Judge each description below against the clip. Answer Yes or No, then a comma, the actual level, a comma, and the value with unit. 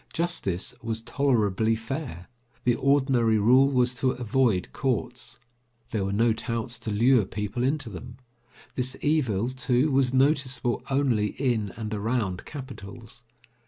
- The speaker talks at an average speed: No, slow, 130 wpm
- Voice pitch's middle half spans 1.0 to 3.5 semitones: Yes, average, 3.2 semitones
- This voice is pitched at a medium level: No, low, 120 Hz